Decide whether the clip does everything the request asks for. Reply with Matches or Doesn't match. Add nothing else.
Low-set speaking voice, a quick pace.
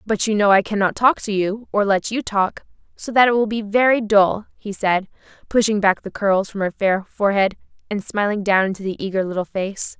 Doesn't match